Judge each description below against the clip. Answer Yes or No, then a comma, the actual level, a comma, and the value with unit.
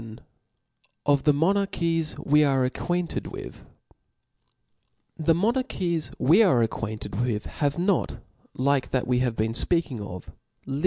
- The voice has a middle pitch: Yes, medium, 145 Hz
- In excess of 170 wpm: No, average, 155 wpm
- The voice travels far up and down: Yes, wide, 5.7 semitones